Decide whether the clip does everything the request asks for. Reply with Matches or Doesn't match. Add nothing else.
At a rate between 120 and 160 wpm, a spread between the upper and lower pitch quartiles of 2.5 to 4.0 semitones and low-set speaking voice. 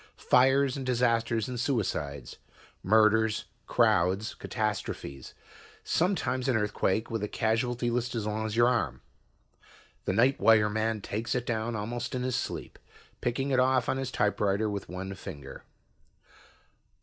Matches